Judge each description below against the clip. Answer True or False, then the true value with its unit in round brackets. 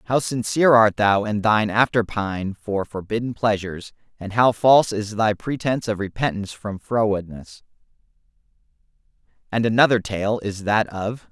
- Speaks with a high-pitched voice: False (110 Hz)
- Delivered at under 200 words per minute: True (145 wpm)